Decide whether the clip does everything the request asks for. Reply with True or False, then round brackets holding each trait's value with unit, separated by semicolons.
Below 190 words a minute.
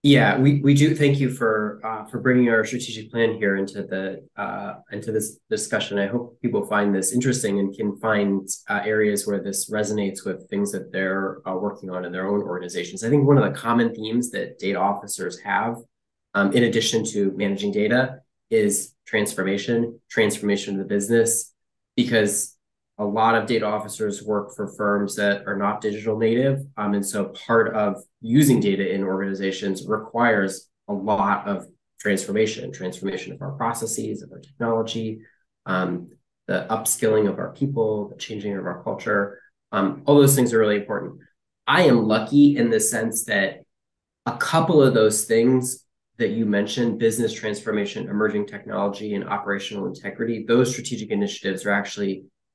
True (170 wpm)